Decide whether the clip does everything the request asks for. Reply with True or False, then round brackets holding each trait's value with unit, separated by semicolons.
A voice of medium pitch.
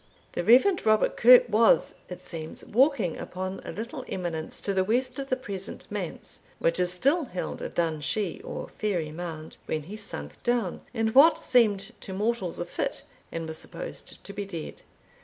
False (200 Hz)